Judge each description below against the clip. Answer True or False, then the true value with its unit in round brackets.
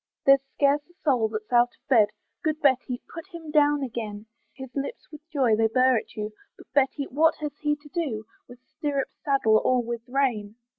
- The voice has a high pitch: True (265 Hz)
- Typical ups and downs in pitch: True (4.1 semitones)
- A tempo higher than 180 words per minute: True (195 wpm)